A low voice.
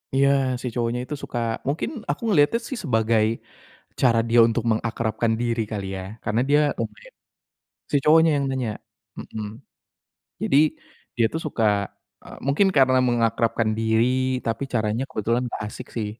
Yes: low, 120 Hz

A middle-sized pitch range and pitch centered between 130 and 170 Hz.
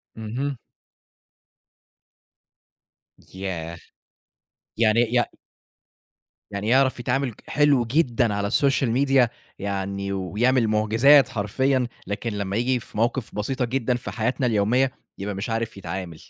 No: average, 4.2 semitones; low, 115 Hz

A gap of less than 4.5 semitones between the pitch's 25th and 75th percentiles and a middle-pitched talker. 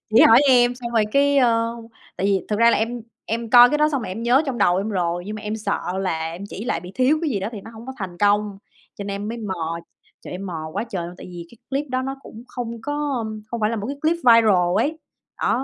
No: average, 3.9 semitones; high, 225 Hz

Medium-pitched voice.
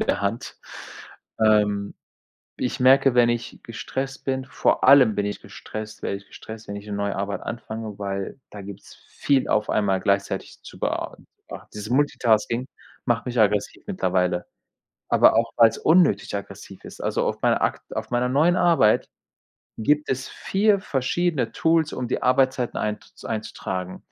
No: low, 115 Hz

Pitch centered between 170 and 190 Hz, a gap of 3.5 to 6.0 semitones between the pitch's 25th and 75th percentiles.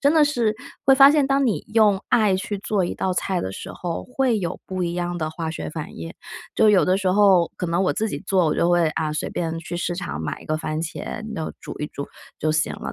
Yes: medium, 185 Hz; average, 4.8 semitones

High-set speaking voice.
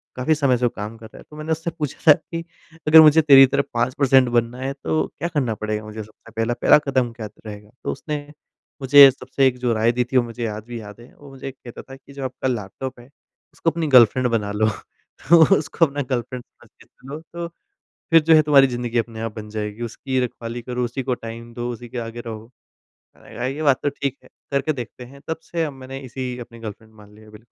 No: low, 125 Hz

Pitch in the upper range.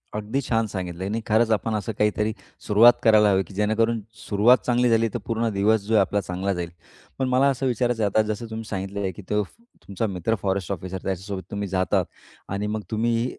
No: low, 105 Hz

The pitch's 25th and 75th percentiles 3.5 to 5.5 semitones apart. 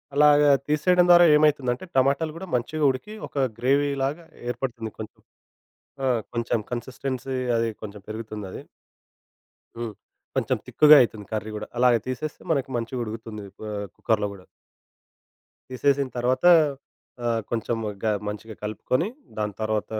Yes: average, 4.5 semitones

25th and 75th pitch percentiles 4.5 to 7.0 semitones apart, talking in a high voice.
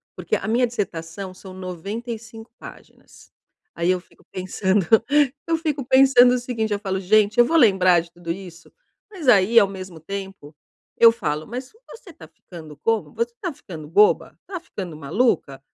Yes: average, 5.3 semitones; high, 200 Hz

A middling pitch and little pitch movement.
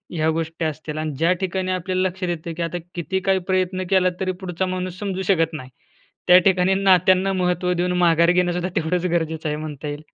Yes: medium, 180 Hz; narrow, 2.3 semitones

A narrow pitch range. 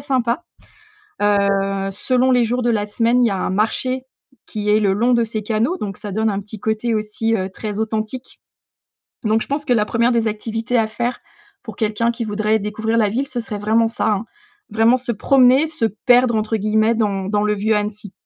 Yes: narrow, 2.3 semitones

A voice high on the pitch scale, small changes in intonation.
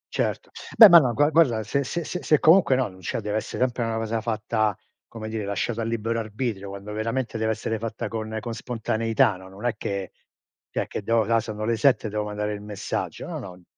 No: low, 110 Hz; narrow, 2.1 semitones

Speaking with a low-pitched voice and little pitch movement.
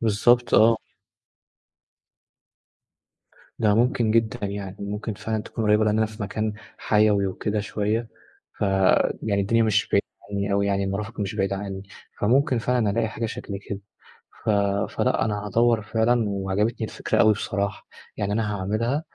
Yes: low, 105 Hz; narrow, 2.0 semitones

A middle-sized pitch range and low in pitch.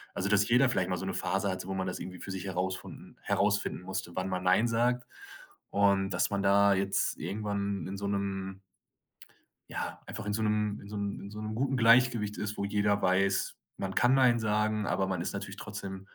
No: narrow, 1.9 semitones; low, 100 Hz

